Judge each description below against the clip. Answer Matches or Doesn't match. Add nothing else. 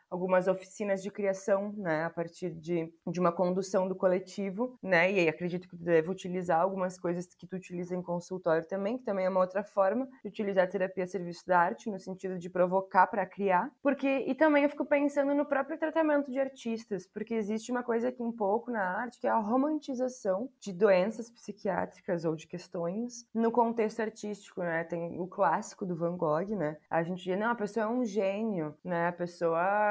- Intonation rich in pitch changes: Doesn't match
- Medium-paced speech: Doesn't match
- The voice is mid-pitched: Doesn't match